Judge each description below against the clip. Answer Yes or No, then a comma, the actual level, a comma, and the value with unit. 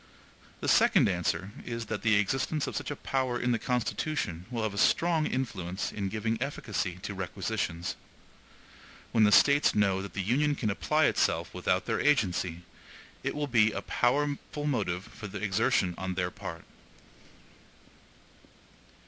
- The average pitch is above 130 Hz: No, low, 110 Hz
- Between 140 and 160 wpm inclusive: Yes, average, 150 wpm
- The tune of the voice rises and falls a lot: Yes, wide, 5.8 semitones